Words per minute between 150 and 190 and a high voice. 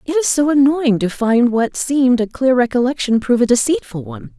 No: fast, 205 wpm; high, 245 Hz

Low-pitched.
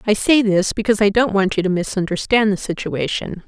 No: high, 200 Hz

